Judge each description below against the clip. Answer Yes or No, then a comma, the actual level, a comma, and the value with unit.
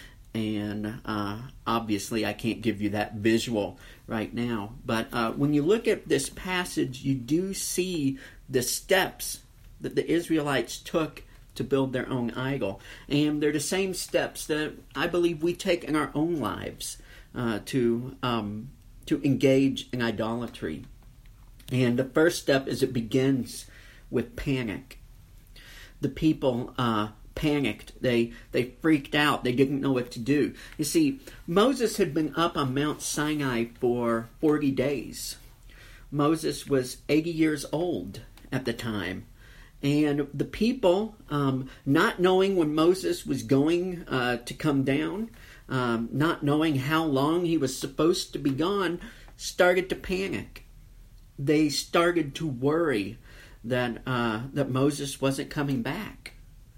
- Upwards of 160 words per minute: No, average, 145 wpm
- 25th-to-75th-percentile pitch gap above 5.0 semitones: No, average, 4.7 semitones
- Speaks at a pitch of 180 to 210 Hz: No, low, 135 Hz